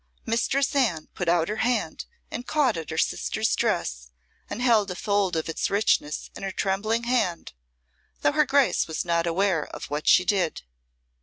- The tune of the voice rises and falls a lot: Yes, wide, 6.0 semitones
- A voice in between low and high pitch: No, high, 195 Hz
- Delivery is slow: No, average, 175 wpm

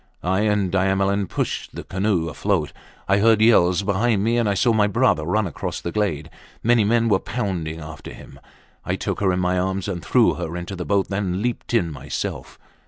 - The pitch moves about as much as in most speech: Yes, average, 3.1 semitones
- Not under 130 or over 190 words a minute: No, average, 200 wpm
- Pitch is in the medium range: No, very low, 95 Hz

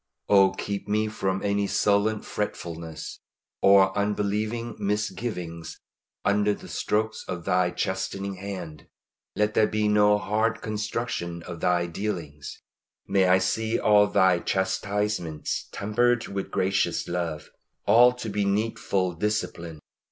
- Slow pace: Yes, slow, 120 wpm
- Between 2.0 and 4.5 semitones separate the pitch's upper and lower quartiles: Yes, average, 2.7 semitones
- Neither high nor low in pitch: No, low, 100 Hz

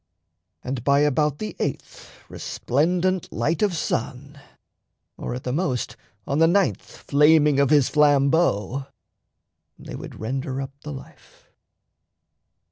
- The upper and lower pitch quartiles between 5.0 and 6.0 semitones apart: No, average, 3.0 semitones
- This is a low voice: No, medium, 145 Hz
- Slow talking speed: Yes, slow, 125 wpm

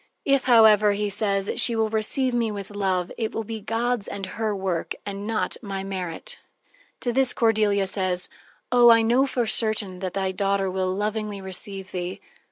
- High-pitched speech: Yes, high, 205 Hz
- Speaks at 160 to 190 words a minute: Yes, average, 175 wpm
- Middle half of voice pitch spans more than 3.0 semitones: No, average, 2.7 semitones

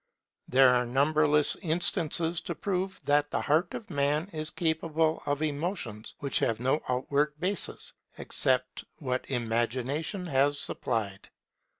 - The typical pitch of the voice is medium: Yes, medium, 150 Hz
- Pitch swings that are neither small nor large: Yes, average, 3.9 semitones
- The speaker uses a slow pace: Yes, slow, 125 wpm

